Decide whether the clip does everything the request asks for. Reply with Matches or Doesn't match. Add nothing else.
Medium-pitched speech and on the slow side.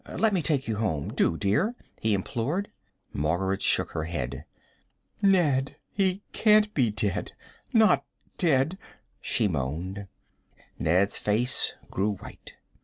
Doesn't match